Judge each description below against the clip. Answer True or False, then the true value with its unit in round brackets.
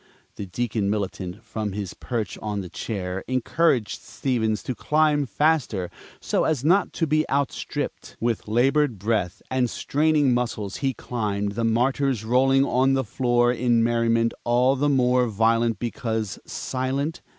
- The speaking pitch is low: True (120 Hz)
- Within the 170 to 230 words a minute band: False (145 wpm)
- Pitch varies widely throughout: False (3.7 semitones)